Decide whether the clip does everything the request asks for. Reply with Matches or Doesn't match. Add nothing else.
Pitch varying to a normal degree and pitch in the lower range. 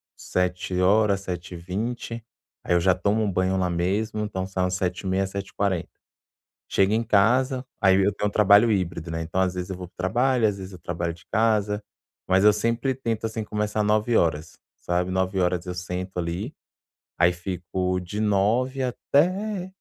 Matches